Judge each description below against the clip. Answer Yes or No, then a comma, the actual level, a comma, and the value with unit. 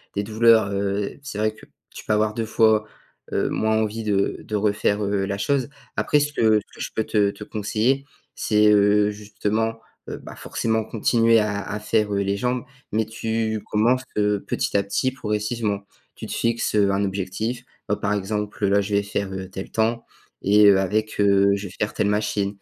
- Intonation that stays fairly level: Yes, narrow, 1.6 semitones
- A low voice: Yes, low, 105 Hz